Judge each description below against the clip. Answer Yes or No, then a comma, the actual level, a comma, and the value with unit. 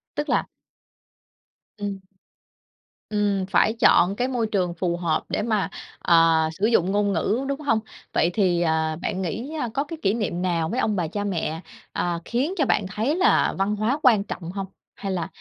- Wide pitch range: No, average, 4.6 semitones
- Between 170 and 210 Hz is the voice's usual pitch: Yes, high, 200 Hz